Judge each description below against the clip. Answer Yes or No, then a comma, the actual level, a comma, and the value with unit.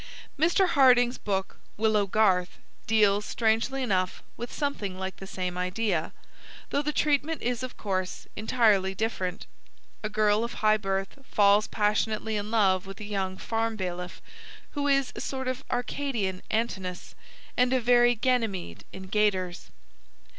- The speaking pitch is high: Yes, high, 215 Hz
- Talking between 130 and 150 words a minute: Yes, average, 145 wpm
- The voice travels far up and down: No, average, 4.4 semitones